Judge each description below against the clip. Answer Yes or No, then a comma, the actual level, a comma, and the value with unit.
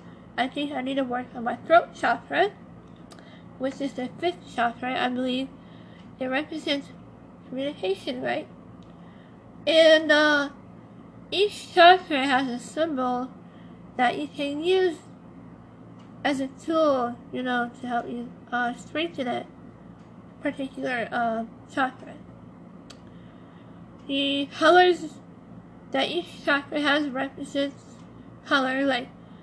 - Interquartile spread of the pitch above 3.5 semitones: No, average, 3.2 semitones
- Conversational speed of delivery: No, slow, 110 wpm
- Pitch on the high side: Yes, very high, 275 Hz